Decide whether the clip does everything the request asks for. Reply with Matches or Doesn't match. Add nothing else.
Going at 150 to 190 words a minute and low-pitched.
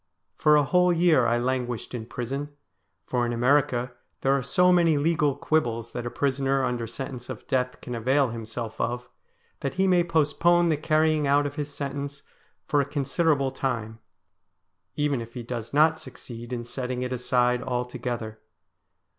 Matches